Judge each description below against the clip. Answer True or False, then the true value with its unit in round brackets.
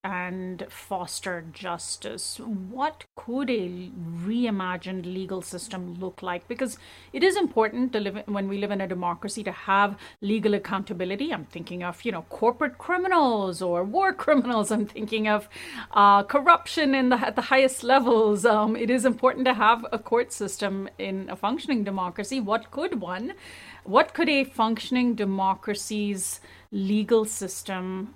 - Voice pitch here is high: True (210 Hz)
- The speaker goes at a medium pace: True (155 wpm)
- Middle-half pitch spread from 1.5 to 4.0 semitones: False (4.6 semitones)